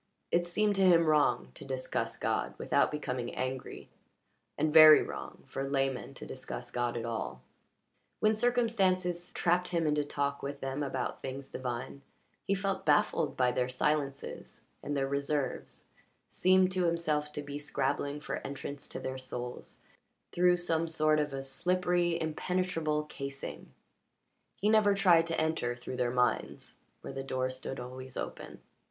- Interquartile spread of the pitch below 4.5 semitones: No, average, 4.8 semitones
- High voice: No, medium, 150 Hz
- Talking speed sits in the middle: Yes, average, 155 wpm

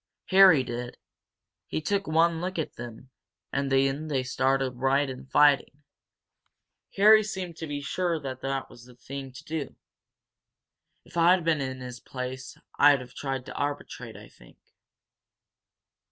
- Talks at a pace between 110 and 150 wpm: Yes, average, 145 wpm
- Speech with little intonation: No, average, 3.8 semitones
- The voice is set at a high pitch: No, medium, 140 Hz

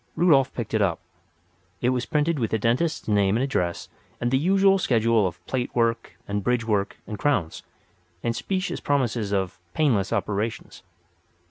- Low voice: Yes, low, 115 Hz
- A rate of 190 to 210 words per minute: No, average, 160 wpm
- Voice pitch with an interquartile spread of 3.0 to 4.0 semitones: No, average, 5.2 semitones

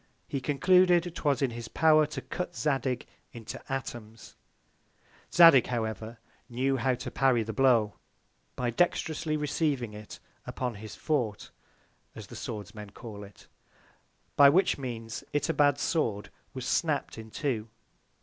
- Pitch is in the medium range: No, low, 130 Hz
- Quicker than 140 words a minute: No, slow, 135 wpm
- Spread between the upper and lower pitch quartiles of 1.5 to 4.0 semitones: No, average, 4.8 semitones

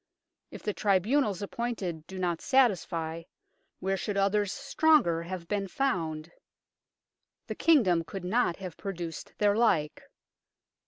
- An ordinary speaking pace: No, slow, 120 wpm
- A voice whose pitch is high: Yes, high, 195 Hz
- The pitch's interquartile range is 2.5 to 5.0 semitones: Yes, average, 4.2 semitones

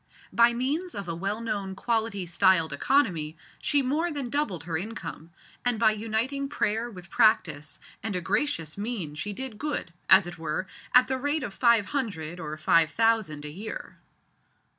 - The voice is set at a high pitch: Yes, high, 210 Hz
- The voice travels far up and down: Yes, wide, 6.6 semitones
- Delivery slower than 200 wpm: Yes, average, 170 wpm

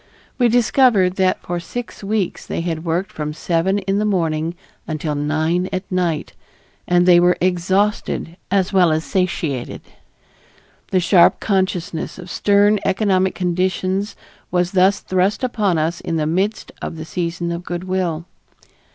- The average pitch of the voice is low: No, medium, 180 Hz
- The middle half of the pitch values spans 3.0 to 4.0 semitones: No, narrow, 2.5 semitones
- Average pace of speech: Yes, average, 150 wpm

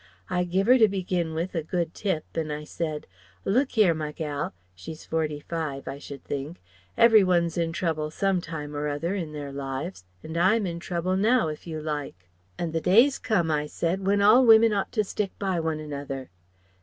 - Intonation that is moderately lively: Yes, average, 4.2 semitones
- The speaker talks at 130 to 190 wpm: No, average, 200 wpm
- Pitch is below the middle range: No, medium, 165 Hz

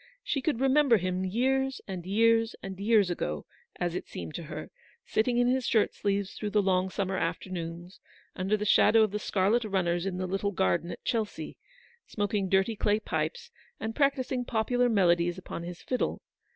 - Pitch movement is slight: No, average, 4.0 semitones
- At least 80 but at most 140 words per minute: No, average, 185 wpm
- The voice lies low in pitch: No, high, 205 Hz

